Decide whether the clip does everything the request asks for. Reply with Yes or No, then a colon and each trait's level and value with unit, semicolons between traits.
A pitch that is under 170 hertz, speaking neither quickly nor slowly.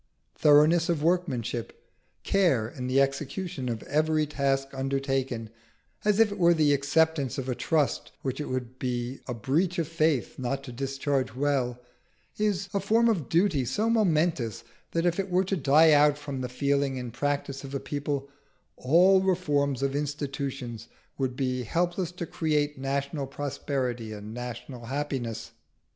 Yes: medium, 140 Hz; average, 155 wpm